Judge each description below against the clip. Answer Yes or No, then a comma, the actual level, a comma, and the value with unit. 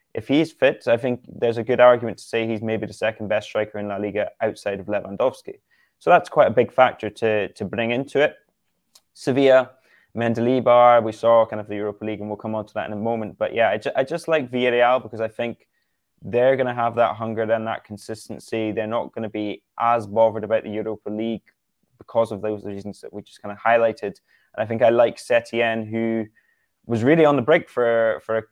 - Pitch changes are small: Yes, narrow, 1.9 semitones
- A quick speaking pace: Yes, fast, 225 wpm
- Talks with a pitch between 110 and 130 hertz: Yes, low, 115 Hz